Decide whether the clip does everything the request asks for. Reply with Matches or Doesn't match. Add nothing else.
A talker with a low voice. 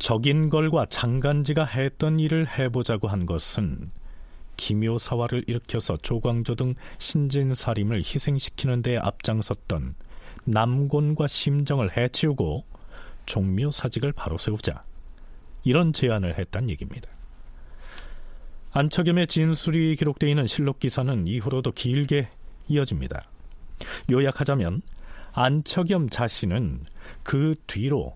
Matches